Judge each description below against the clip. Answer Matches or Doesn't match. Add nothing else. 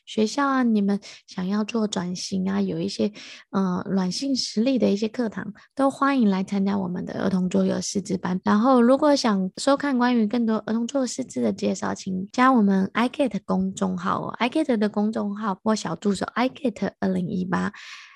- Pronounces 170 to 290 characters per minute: Doesn't match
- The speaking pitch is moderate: Doesn't match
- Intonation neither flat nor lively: Matches